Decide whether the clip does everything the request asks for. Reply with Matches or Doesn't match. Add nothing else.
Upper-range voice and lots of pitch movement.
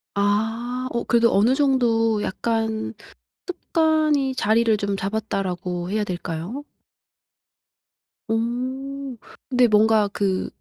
Doesn't match